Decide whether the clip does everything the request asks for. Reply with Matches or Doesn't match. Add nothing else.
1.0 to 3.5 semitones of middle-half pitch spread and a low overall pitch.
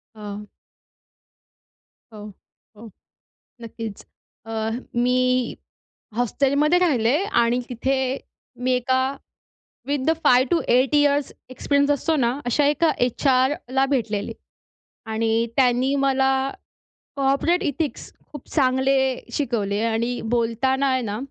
Doesn't match